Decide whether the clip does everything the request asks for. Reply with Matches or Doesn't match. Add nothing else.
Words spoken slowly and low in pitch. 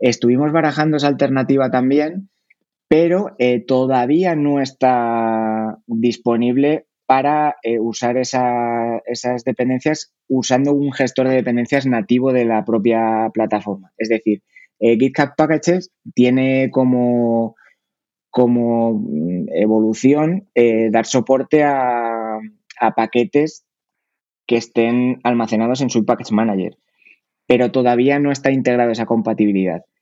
Matches